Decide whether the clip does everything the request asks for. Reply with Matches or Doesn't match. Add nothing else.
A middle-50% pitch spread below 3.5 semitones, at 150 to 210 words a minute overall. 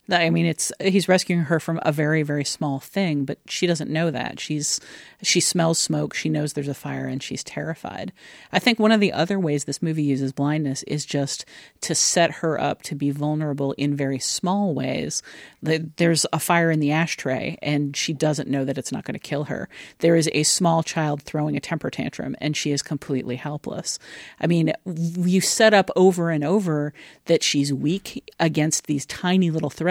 Matches